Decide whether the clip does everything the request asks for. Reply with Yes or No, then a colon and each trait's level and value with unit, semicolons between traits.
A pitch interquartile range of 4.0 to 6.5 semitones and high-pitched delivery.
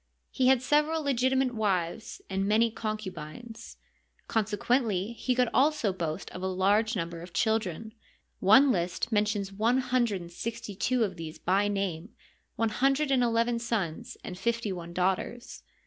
Yes: average, 4.5 semitones; high, 220 Hz